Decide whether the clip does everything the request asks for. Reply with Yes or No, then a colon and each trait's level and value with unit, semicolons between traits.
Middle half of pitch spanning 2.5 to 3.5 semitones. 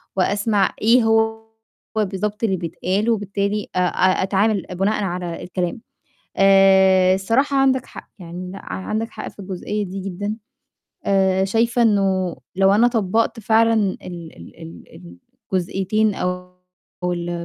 Yes: average, 2.8 semitones